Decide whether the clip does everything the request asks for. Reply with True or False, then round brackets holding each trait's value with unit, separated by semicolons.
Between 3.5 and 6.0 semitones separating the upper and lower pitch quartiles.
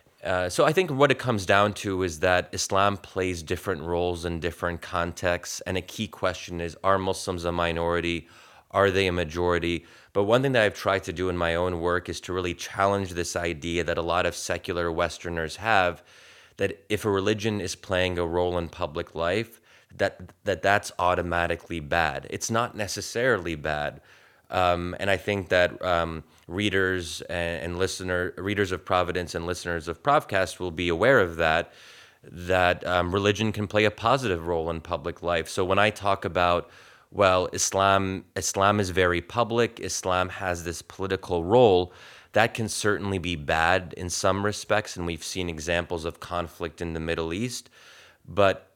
False (2.4 semitones)